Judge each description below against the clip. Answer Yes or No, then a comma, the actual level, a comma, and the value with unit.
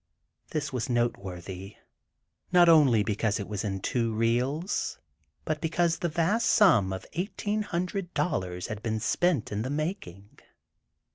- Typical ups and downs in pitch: No, wide, 8.8 semitones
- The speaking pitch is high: No, low, 120 Hz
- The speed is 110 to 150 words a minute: Yes, average, 140 wpm